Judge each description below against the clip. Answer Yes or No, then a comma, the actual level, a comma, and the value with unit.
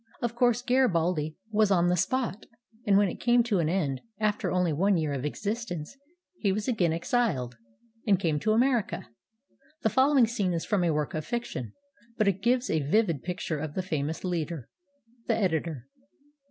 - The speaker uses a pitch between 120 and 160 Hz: No, medium, 185 Hz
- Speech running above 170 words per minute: Yes, average, 180 wpm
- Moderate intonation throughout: No, wide, 6.0 semitones